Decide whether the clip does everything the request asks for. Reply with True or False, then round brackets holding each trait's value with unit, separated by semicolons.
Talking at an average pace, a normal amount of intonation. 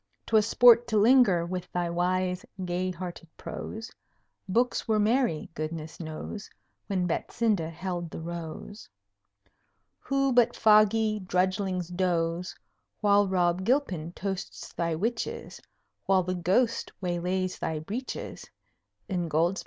False (115 wpm; 3.8 semitones)